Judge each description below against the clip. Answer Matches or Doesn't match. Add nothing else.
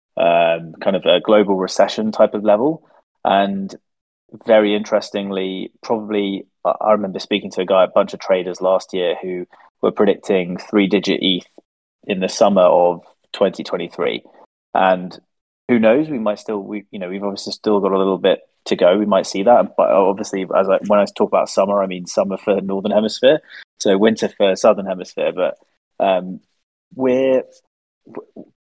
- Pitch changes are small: Matches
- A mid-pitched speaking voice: Doesn't match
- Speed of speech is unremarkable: Matches